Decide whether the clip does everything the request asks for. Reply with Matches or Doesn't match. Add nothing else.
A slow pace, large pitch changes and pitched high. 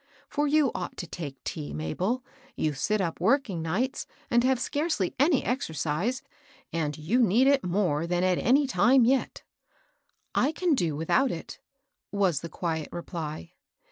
Doesn't match